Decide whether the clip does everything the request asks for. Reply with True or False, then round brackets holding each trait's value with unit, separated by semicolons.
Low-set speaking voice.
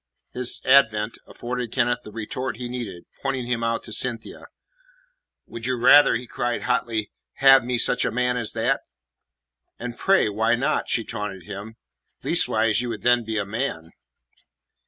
True (120 Hz)